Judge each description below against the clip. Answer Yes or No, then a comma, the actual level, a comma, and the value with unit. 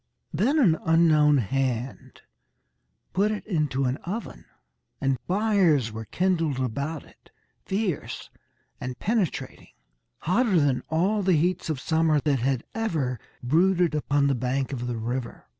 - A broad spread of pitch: Yes, wide, 5.8 semitones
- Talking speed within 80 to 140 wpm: Yes, slow, 135 wpm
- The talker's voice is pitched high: No, medium, 155 Hz